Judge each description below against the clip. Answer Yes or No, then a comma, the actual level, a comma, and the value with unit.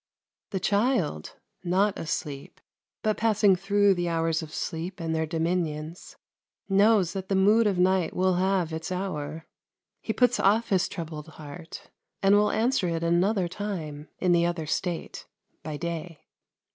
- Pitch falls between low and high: Yes, medium, 180 Hz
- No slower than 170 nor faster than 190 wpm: No, average, 150 wpm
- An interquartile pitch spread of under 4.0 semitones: Yes, average, 3.5 semitones